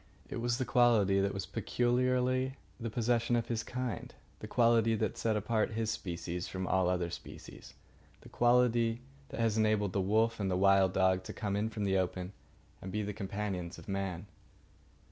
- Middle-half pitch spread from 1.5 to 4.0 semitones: Yes, average, 3.5 semitones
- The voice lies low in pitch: Yes, low, 110 Hz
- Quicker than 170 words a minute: Yes, average, 185 wpm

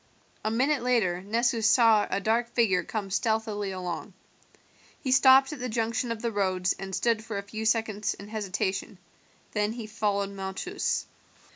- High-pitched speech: Yes, high, 220 Hz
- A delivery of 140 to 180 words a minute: Yes, average, 160 wpm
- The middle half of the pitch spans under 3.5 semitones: Yes, average, 2.8 semitones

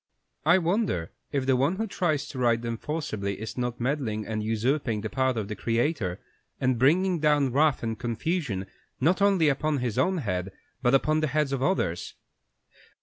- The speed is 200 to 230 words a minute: No, average, 180 wpm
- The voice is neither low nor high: No, low, 130 Hz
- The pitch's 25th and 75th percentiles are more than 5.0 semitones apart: Yes, wide, 5.4 semitones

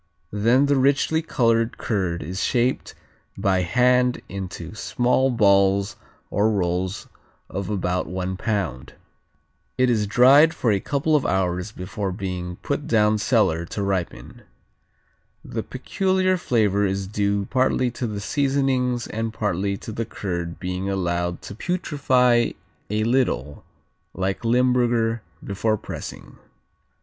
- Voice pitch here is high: No, low, 105 Hz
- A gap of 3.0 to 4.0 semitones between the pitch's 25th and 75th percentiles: No, average, 4.8 semitones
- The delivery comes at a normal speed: No, slow, 125 wpm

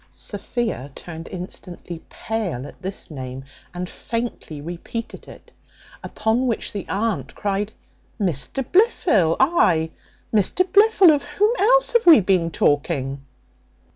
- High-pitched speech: Yes, high, 200 Hz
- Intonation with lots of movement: Yes, wide, 7.6 semitones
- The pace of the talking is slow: Yes, slow, 120 wpm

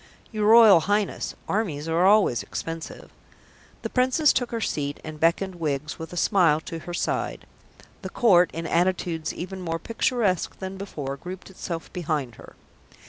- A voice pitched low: No, medium, 175 Hz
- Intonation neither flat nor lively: Yes, average, 3.9 semitones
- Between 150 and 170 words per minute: Yes, average, 155 wpm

